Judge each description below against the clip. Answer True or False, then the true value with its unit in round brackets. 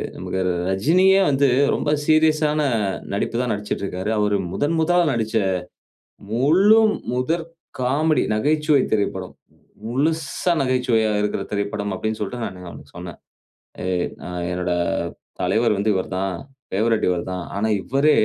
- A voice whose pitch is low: True (115 Hz)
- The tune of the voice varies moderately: False (7.0 semitones)